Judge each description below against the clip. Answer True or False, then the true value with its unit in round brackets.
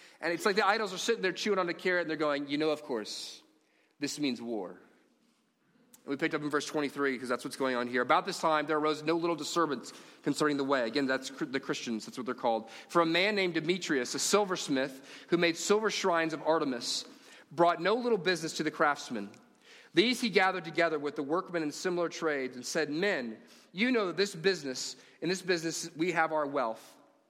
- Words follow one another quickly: True (215 wpm)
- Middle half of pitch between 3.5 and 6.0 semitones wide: True (4.3 semitones)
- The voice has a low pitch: False (160 Hz)